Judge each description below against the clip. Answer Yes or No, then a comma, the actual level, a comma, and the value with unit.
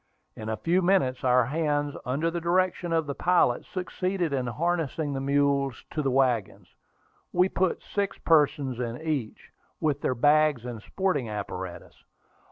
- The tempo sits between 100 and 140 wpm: No, average, 155 wpm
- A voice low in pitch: No, medium, 145 Hz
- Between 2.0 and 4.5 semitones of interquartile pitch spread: No, average, 5.1 semitones